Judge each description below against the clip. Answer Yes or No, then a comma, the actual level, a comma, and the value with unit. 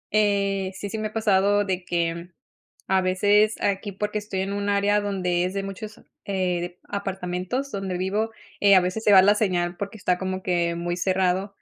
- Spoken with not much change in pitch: Yes, narrow, 2.0 semitones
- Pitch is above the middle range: Yes, high, 195 Hz